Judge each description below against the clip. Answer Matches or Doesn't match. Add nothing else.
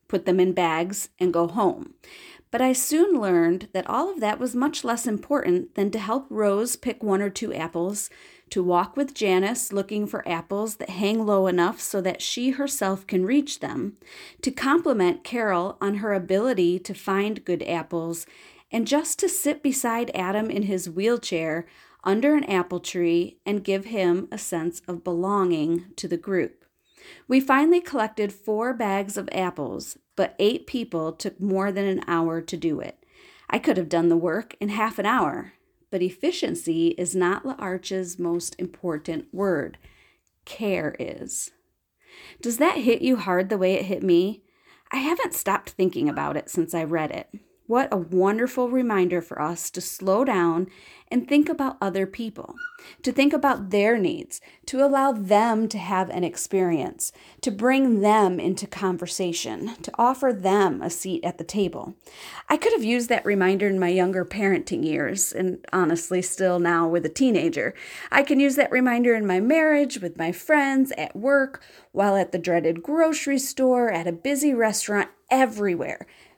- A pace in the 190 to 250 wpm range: Doesn't match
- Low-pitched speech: Doesn't match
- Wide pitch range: Matches